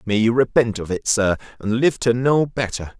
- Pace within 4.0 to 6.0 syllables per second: Yes, 4.9 syllables/s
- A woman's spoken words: No, male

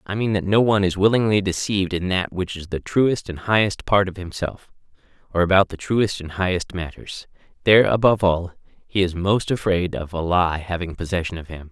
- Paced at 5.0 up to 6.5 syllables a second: Yes, 5.5 syllables/s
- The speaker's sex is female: No, male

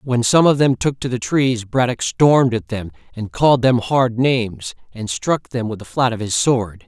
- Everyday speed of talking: No, fast, 235 wpm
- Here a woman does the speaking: No, male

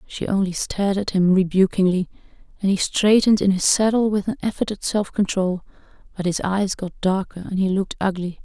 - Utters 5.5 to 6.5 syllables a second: Yes, 5.6 syllables/s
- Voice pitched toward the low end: No, high, 195 Hz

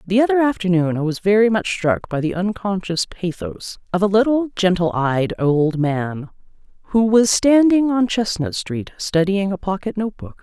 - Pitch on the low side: No, high, 190 Hz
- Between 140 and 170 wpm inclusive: Yes, average, 165 wpm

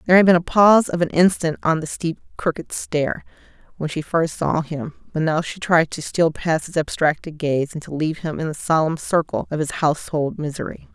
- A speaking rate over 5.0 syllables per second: Yes, 5.3 syllables/s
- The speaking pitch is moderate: Yes, medium, 160 Hz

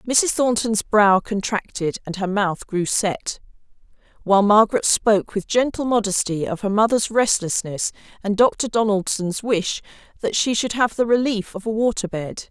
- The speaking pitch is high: Yes, high, 210 Hz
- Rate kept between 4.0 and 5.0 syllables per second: Yes, 4.7 syllables/s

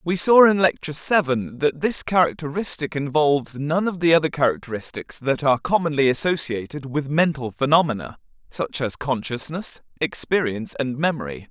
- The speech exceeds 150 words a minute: No, average, 140 wpm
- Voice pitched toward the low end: No, medium, 145 Hz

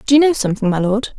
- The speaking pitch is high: Yes, high, 235 Hz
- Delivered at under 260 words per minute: No, fast, 305 wpm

